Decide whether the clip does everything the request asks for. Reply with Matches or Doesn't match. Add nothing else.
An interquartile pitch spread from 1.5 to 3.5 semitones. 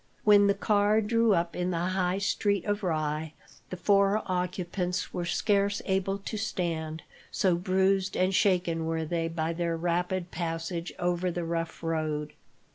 Matches